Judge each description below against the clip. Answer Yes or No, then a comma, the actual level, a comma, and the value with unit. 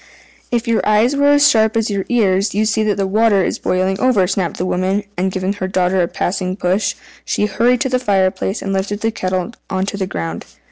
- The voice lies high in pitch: Yes, high, 195 Hz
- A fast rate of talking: Yes, fast, 230 wpm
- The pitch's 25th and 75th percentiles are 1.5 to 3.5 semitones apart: Yes, average, 2.9 semitones